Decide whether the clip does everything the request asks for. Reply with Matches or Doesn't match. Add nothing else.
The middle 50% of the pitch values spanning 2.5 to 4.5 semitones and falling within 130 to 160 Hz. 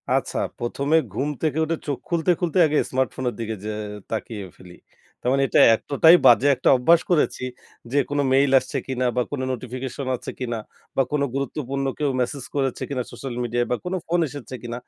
Matches